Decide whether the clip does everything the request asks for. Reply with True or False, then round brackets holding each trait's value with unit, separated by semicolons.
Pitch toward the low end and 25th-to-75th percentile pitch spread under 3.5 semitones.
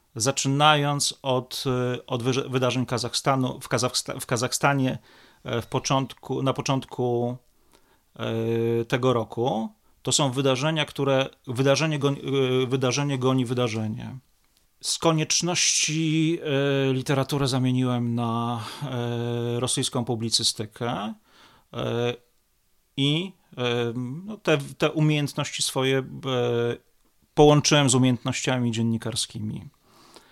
True (130 Hz; 2.8 semitones)